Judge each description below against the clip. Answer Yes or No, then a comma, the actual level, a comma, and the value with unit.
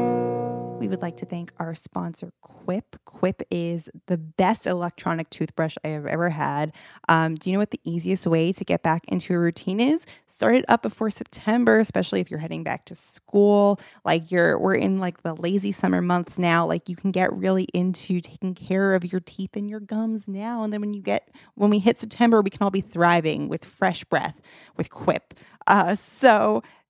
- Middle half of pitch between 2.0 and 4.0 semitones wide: Yes, average, 3.6 semitones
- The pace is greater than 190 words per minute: Yes, fast, 205 wpm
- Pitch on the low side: No, medium, 180 Hz